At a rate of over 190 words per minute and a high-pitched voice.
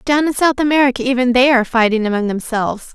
Yes: fast, 205 wpm; very high, 250 Hz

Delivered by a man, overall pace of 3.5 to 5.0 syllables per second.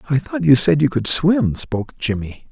Yes: male; 4.9 syllables/s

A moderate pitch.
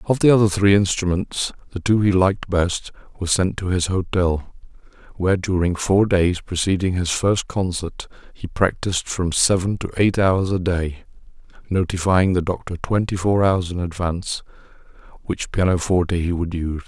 No: very low, 95 Hz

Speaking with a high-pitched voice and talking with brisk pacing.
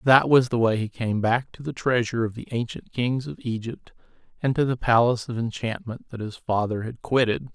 No: low, 120 Hz; fast, 215 wpm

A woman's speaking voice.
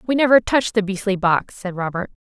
Yes: female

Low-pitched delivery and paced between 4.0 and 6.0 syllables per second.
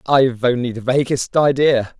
Yes: low, 130 Hz; 4.9 syllables/s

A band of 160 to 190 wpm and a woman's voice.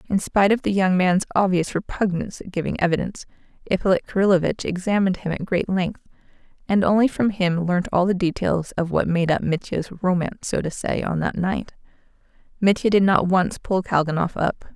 Yes: average, 185 wpm; female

